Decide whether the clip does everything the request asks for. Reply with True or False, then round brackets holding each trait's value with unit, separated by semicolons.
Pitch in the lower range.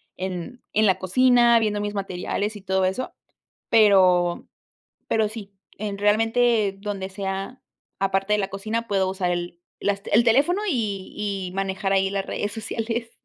False (200 Hz)